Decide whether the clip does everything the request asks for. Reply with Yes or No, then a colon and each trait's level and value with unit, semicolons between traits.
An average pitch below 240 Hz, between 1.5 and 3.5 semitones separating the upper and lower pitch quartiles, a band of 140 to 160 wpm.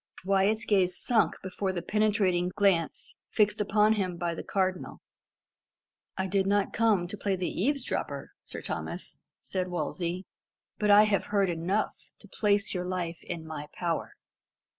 Yes: high, 190 Hz; average, 2.8 semitones; average, 150 wpm